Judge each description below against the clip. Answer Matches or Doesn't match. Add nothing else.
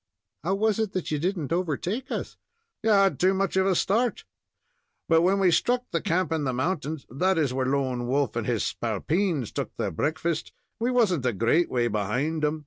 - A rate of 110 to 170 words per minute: Doesn't match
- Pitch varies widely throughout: Matches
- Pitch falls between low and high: Matches